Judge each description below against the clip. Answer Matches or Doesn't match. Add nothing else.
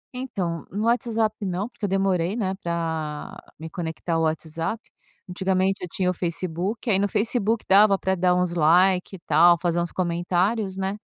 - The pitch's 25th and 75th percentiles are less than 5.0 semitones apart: Matches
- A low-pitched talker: Doesn't match